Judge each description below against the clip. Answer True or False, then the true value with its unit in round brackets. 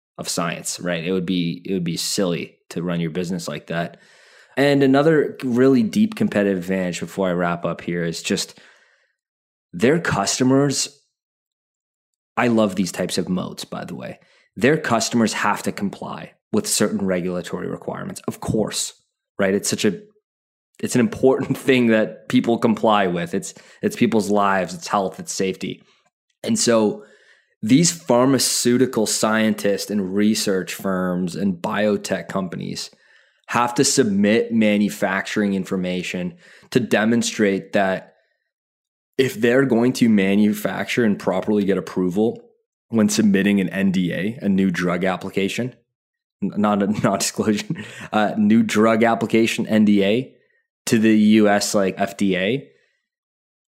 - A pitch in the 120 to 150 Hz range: False (105 Hz)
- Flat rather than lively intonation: False (4.4 semitones)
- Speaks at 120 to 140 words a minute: True (135 wpm)